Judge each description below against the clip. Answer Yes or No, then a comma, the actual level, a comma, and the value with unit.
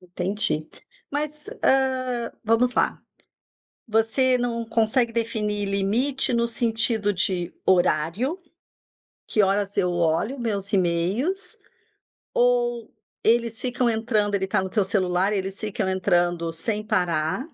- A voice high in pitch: Yes, high, 215 Hz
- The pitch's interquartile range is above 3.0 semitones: Yes, average, 4.1 semitones